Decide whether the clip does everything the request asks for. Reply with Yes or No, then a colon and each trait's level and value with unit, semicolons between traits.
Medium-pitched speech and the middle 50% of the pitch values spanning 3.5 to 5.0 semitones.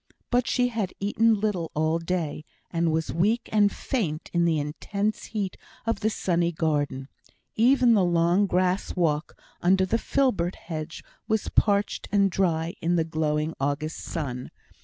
Yes: medium, 175 Hz; average, 4.5 semitones